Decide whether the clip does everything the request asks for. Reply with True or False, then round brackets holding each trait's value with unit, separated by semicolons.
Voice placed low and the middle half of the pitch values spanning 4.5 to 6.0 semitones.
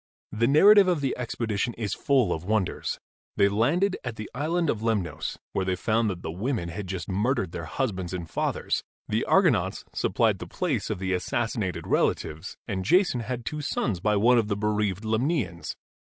True (110 Hz; 5.0 semitones)